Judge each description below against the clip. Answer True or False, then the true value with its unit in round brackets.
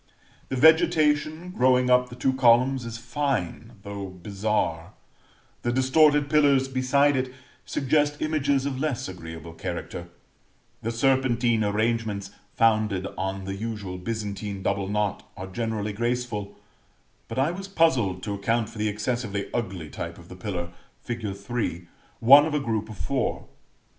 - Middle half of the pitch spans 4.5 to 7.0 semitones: True (4.9 semitones)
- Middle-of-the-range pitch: False (115 Hz)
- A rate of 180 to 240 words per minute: False (145 wpm)